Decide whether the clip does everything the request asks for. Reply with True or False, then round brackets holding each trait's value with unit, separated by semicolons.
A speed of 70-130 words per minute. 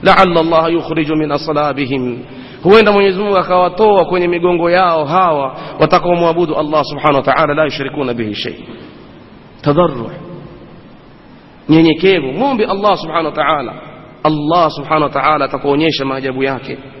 True (125 wpm)